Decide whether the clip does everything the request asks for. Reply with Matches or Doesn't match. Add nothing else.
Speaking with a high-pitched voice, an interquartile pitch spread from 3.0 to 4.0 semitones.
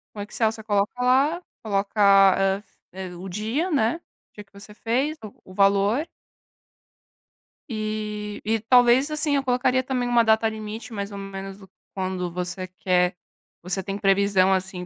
Matches